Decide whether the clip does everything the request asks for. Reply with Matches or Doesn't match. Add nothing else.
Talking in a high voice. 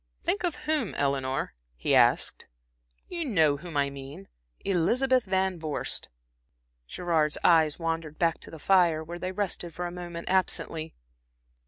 Doesn't match